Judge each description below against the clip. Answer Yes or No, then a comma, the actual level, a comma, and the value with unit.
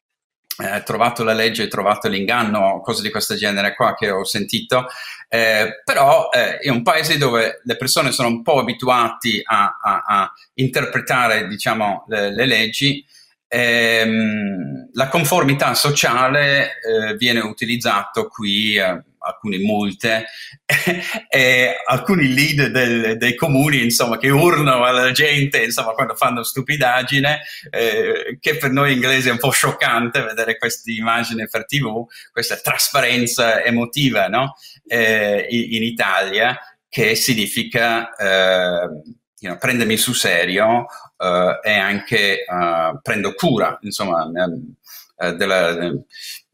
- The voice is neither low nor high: No, low, 120 Hz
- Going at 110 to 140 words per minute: Yes, average, 130 wpm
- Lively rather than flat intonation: No, average, 3.9 semitones